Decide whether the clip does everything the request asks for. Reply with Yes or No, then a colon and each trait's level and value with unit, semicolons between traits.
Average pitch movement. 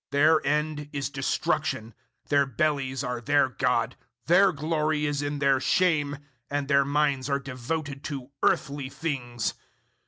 No: narrow, 2.0 semitones